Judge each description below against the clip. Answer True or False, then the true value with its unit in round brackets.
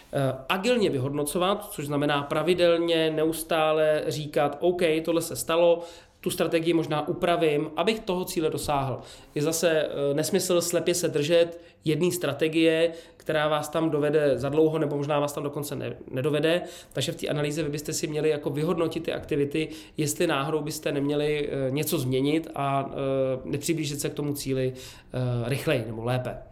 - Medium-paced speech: True (150 wpm)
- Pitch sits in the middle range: True (155 Hz)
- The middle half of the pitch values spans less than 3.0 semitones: True (2.5 semitones)